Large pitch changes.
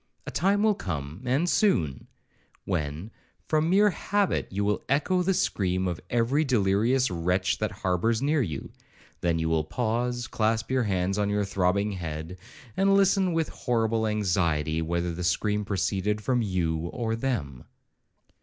Yes: wide, 6.5 semitones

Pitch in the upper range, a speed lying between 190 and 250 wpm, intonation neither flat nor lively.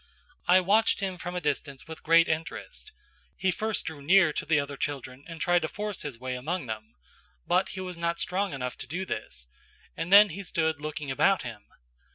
No: medium, 165 Hz; average, 200 wpm; average, 4.7 semitones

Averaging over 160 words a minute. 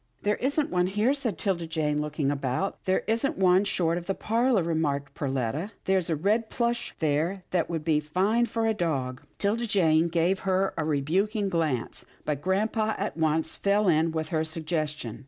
Yes: average, 190 wpm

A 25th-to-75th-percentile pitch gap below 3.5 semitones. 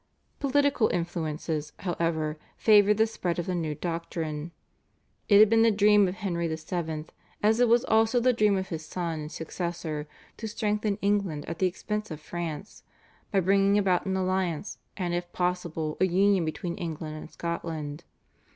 No: average, 4.1 semitones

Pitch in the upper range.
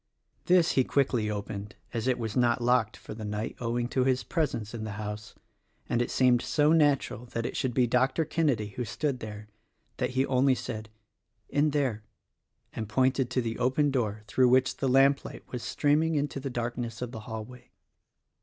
No: low, 125 Hz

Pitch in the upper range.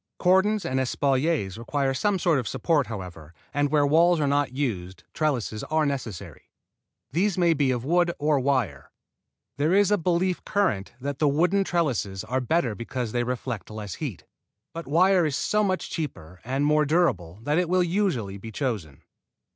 No: medium, 145 Hz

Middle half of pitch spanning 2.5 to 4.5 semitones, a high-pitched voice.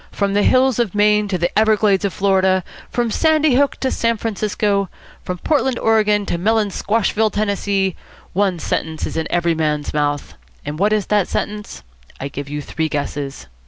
Yes: average, 4.0 semitones; high, 200 Hz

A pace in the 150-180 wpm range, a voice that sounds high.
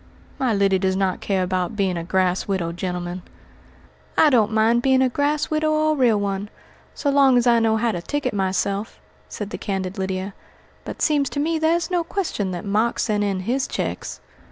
No: average, 200 wpm; high, 210 Hz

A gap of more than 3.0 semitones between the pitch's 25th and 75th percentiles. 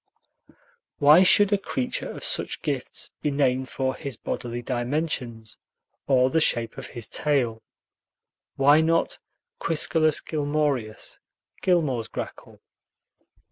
Yes: average, 4.1 semitones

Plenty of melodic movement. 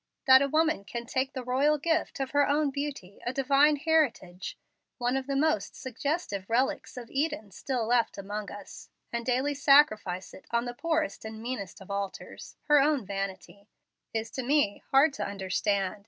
Yes: wide, 5.8 semitones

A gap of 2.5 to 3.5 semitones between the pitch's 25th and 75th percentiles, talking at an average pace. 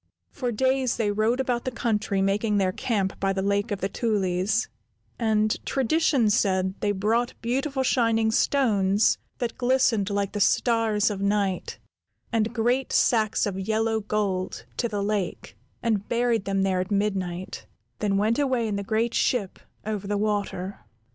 Yes: average, 2.9 semitones; average, 160 wpm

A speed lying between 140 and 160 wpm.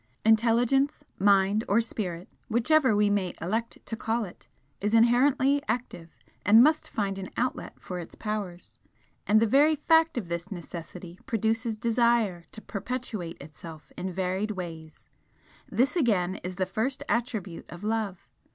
Yes: average, 145 wpm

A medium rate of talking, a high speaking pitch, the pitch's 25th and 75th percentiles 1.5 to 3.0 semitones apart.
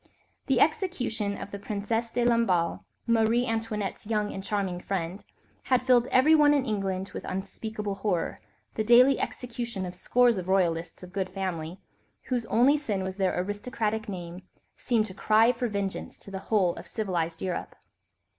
No: average, 160 wpm; high, 210 Hz; average, 3.9 semitones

